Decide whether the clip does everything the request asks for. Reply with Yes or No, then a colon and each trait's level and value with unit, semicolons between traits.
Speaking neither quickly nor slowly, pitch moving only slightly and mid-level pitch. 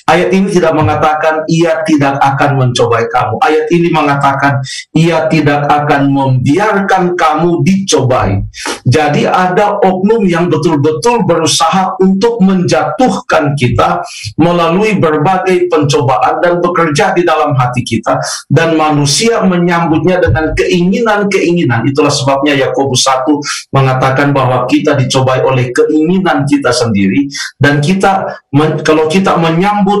No: average, 115 wpm; average, 3.9 semitones; medium, 155 Hz